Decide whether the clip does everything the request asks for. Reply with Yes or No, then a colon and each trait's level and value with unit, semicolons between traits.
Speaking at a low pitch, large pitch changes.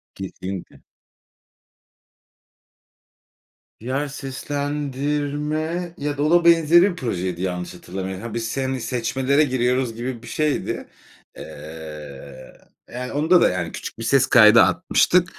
Yes: low, 130 Hz; wide, 7.3 semitones